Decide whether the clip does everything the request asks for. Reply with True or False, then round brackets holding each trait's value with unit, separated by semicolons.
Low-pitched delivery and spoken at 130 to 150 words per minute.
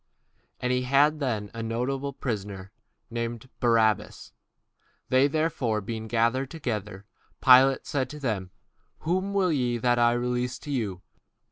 True (125 Hz; 140 wpm)